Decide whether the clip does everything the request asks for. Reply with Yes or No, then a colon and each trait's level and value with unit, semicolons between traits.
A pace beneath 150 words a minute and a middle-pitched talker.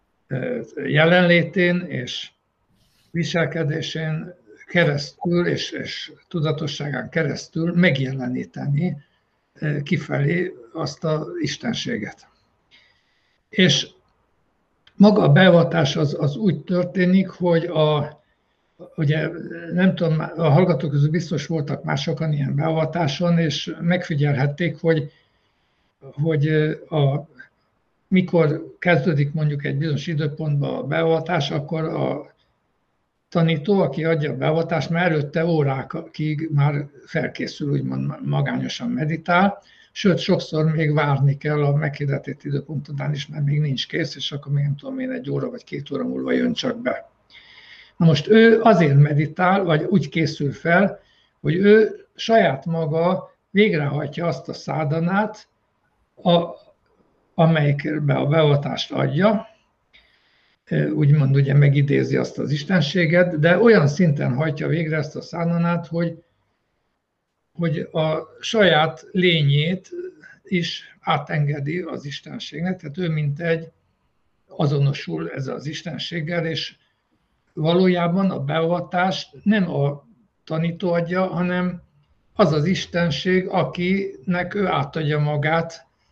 Yes: average, 110 wpm; medium, 160 Hz